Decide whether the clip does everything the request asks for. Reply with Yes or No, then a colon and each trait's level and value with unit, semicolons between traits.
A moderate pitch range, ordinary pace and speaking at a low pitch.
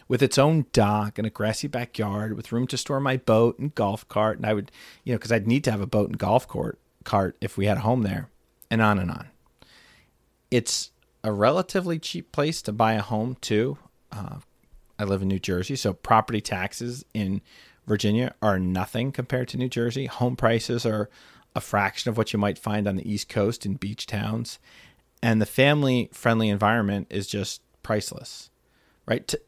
Yes: average, 3.2 semitones; average, 195 wpm; low, 110 Hz